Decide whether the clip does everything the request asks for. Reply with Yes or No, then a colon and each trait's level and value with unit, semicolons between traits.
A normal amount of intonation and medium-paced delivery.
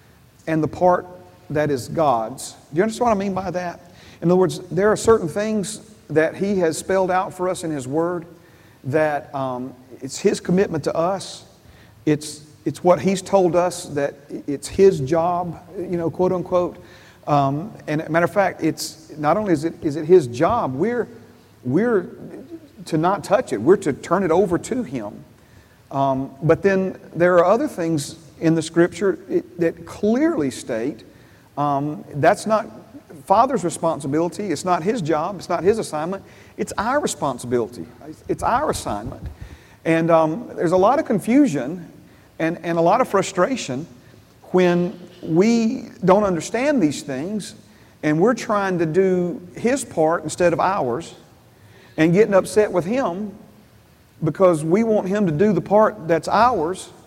Yes: average, 4.0 semitones; average, 165 wpm